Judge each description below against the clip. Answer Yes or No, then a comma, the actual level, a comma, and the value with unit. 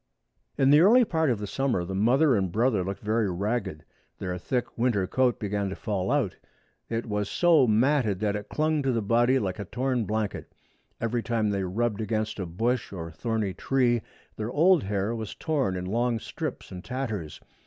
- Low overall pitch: Yes, low, 110 Hz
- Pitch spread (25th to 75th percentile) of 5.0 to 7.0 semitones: No, average, 4.2 semitones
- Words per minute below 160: No, average, 190 wpm